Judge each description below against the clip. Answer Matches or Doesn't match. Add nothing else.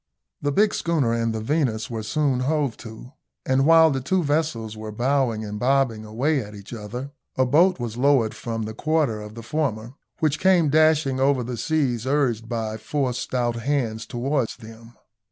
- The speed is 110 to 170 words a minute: Doesn't match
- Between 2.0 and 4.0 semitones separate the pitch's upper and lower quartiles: Doesn't match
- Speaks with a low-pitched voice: Matches